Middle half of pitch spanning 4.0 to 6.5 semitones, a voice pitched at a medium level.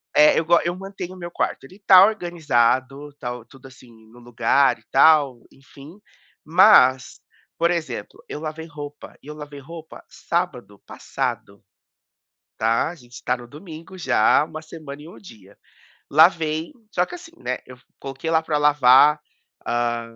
Yes: average, 4.8 semitones; medium, 150 Hz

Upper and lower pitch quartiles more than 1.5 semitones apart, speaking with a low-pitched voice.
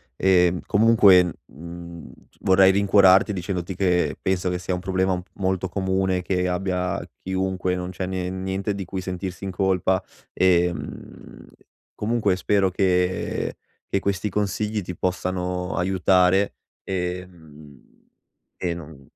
No: narrow, 1.1 semitones; very low, 95 Hz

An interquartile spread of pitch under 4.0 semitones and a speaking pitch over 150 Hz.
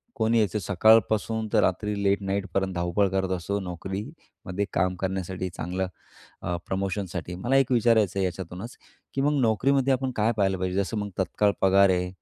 No: average, 2.9 semitones; low, 100 Hz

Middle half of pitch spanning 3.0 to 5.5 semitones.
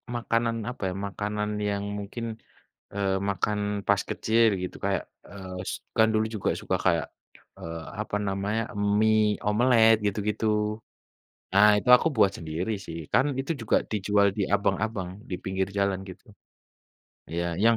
No: narrow, 2.5 semitones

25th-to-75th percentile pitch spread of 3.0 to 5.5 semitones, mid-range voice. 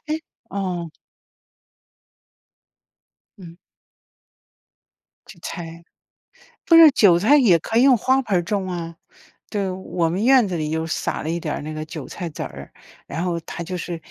Yes: average, 3.9 semitones; medium, 175 Hz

